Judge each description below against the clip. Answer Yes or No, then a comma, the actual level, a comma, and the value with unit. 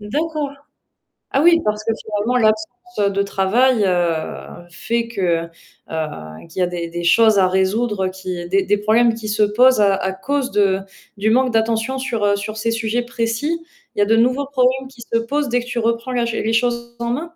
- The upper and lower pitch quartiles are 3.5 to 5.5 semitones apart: Yes, average, 4.0 semitones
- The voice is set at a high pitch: Yes, high, 225 Hz